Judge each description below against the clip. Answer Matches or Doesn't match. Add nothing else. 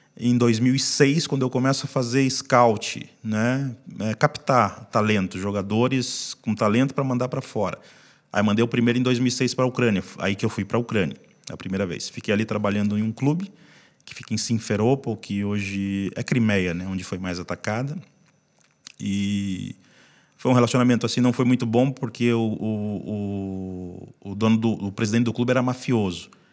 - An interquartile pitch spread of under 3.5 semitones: Doesn't match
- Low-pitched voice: Matches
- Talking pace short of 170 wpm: Doesn't match